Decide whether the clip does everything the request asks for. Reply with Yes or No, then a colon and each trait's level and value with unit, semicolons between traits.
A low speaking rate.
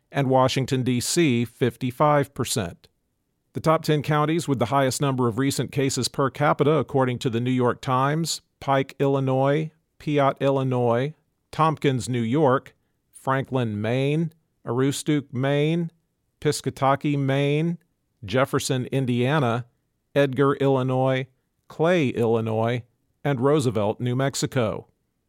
Yes: slow, 110 wpm